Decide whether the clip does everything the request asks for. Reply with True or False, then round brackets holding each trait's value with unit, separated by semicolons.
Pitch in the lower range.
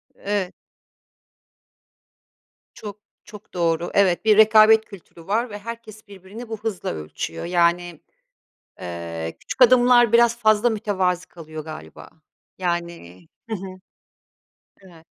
False (195 Hz)